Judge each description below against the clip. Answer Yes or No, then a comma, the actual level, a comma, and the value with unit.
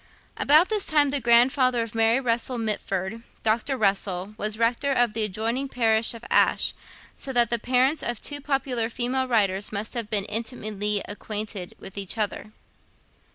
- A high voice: Yes, high, 230 Hz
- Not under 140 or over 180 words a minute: Yes, average, 160 wpm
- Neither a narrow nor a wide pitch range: Yes, average, 3.2 semitones